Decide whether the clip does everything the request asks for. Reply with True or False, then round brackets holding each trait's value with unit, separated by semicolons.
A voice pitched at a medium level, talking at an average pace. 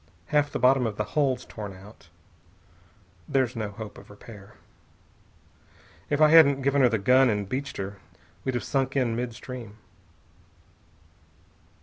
False (125 Hz; 145 wpm)